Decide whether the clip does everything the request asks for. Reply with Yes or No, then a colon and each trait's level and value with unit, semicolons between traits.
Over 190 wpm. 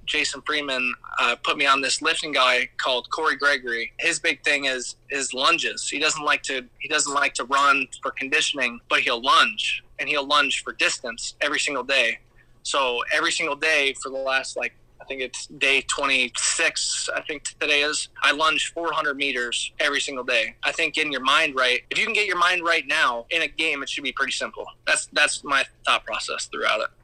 Yes: fast, 205 wpm